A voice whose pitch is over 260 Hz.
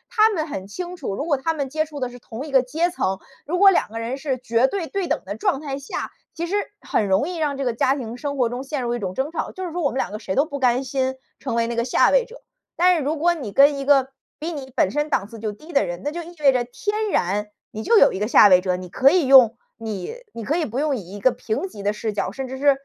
Yes: very high, 270 Hz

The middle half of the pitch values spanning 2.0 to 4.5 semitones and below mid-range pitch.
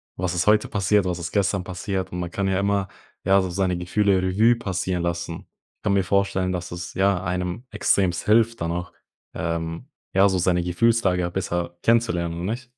Yes: narrow, 2.4 semitones; very low, 95 Hz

